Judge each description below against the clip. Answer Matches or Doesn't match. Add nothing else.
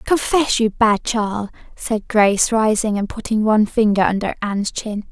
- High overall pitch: Matches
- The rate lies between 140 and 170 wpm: Matches